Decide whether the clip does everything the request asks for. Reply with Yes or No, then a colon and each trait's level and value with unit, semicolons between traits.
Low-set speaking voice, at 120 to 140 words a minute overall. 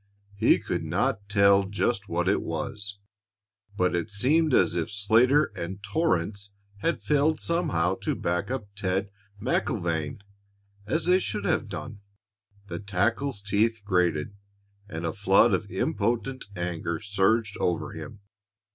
Yes: low, 100 Hz; slow, 135 wpm